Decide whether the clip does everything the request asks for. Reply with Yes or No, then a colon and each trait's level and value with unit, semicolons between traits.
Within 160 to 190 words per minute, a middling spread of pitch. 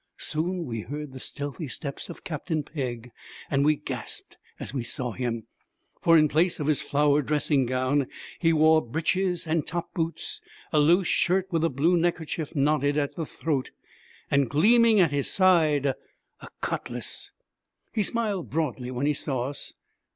Yes: average, 165 wpm; average, 3.3 semitones